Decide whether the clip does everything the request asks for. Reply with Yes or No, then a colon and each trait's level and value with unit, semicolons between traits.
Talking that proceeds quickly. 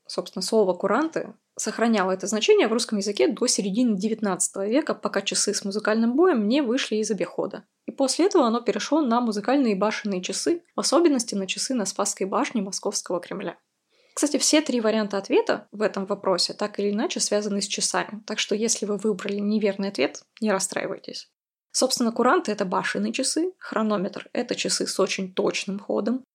Yes: fast, 170 wpm